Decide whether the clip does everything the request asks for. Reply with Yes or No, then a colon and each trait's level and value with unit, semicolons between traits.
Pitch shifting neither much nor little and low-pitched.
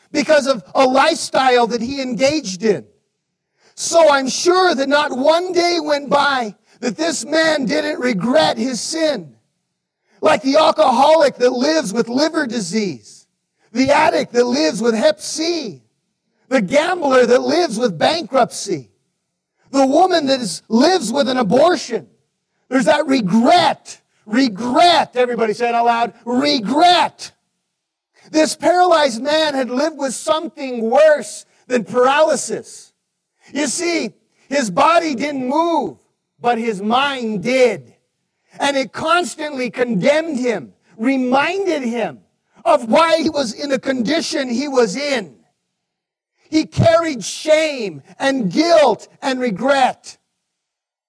No: average, 4.6 semitones; very high, 270 Hz